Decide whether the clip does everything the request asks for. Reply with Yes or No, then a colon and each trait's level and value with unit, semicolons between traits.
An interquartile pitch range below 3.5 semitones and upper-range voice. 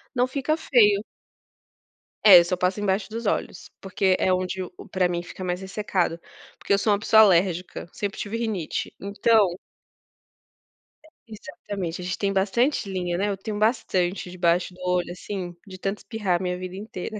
Yes: narrow, 2.6 semitones; high, 195 Hz